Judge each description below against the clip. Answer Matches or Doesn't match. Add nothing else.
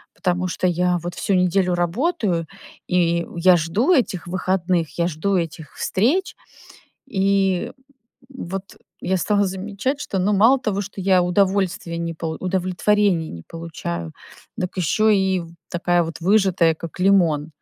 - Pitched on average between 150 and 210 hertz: Matches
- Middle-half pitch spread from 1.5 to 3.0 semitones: Matches